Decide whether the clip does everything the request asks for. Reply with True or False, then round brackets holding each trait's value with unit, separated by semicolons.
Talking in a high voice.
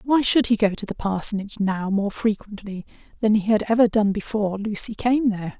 True (210 Hz)